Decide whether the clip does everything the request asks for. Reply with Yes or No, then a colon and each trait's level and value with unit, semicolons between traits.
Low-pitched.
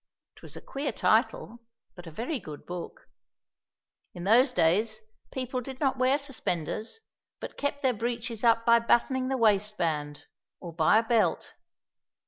No: high, 230 Hz